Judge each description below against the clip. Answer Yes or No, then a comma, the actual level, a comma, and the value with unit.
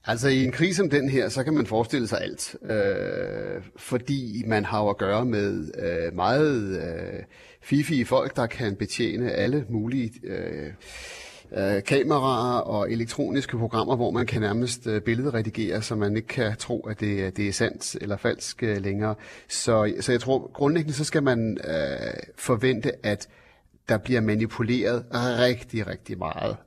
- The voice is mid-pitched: No, low, 120 Hz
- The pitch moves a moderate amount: Yes, average, 3.6 semitones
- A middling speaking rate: Yes, average, 165 wpm